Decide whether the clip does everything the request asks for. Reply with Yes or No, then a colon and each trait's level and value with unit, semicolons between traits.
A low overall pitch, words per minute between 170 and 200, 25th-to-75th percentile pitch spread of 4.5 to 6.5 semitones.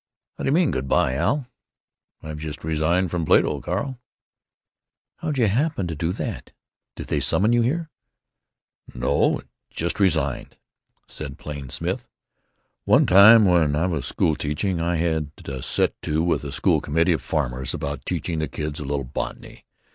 No: very low, 80 Hz; average, 160 wpm; average, 4.8 semitones